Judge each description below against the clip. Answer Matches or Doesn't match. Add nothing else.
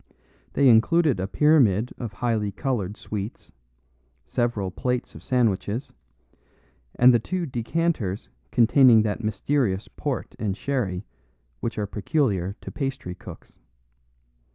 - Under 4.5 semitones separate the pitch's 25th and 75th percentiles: Doesn't match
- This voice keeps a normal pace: Doesn't match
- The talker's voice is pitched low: Matches